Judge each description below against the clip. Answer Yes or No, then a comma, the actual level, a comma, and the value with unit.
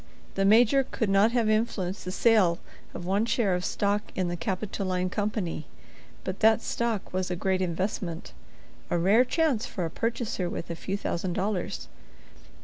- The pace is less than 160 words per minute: No, average, 165 wpm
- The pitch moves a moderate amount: Yes, average, 3.4 semitones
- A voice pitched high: Yes, high, 195 Hz